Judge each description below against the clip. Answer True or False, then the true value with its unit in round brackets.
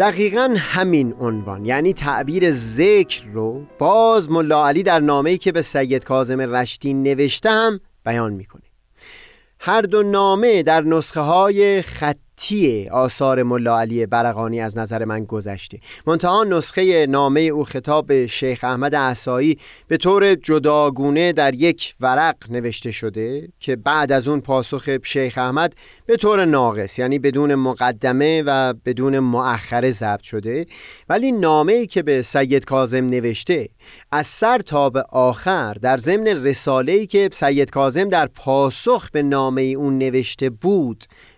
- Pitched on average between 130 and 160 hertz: True (140 Hz)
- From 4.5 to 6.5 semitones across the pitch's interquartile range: True (5.1 semitones)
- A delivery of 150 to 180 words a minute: False (140 wpm)